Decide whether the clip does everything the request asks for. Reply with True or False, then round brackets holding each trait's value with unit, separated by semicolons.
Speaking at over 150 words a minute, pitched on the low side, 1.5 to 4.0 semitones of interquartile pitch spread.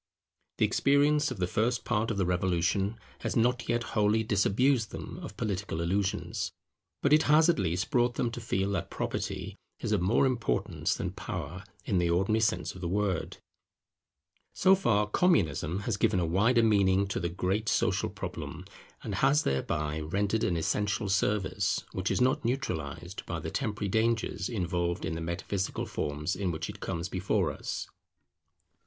False (170 wpm; 100 Hz; 4.5 semitones)